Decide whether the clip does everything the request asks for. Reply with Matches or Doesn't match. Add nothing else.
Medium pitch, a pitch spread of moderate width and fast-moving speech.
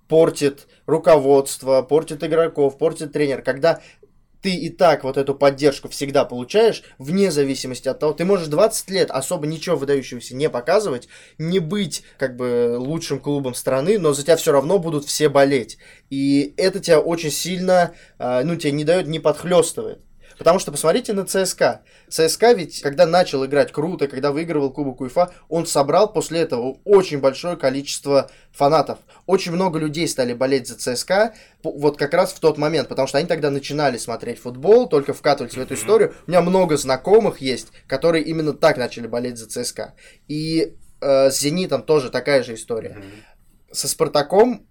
Matches